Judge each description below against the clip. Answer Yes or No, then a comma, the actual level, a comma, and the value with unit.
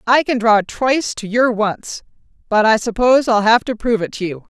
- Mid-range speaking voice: No, high, 225 Hz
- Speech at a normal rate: No, fast, 220 wpm